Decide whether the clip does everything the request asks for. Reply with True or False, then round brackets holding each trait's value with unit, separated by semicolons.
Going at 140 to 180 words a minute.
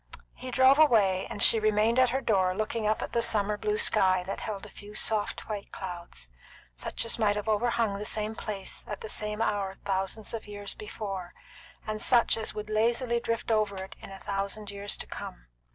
False (200 wpm)